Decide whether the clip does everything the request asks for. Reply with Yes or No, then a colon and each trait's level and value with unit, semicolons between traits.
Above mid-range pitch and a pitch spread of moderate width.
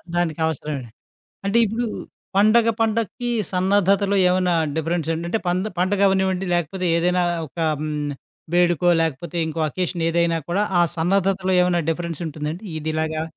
No: medium, 175 Hz; average, 3.0 semitones